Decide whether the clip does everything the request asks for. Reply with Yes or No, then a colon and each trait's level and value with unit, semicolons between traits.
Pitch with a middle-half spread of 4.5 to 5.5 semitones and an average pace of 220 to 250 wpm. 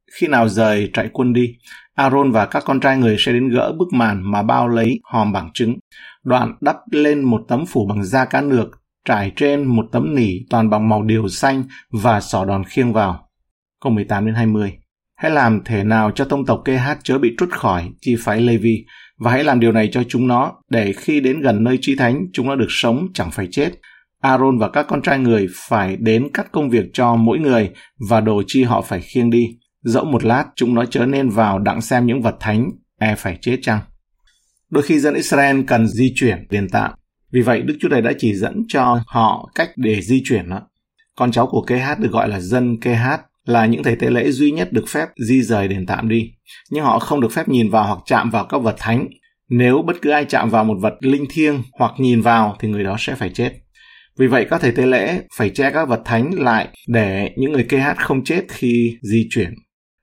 No: average, 3.2 semitones; average, 230 wpm